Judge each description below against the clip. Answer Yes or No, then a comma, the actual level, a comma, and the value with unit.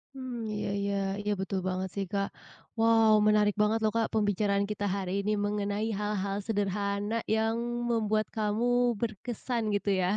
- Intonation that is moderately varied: No, narrow, 1.6 semitones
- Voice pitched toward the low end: No, high, 210 Hz